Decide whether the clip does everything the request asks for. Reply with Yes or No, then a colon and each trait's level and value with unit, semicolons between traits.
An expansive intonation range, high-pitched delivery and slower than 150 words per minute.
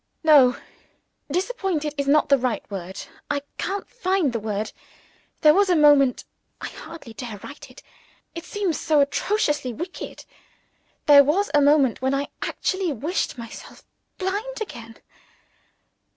Yes: wide, 5.9 semitones; very high, 295 Hz; slow, 135 wpm